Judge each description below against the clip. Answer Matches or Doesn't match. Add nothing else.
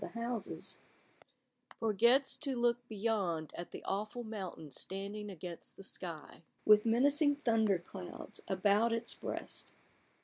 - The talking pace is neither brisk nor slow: Doesn't match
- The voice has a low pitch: Doesn't match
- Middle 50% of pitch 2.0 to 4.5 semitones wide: Matches